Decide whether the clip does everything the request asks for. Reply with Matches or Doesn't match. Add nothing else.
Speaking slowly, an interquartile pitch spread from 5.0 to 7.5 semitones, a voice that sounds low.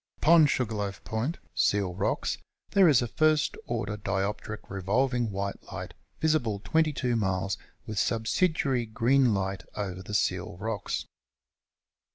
Matches